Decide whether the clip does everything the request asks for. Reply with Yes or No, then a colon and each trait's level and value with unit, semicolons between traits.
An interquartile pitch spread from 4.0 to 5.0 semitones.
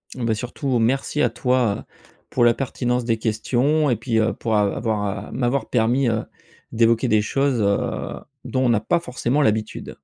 No: average, 2.7 semitones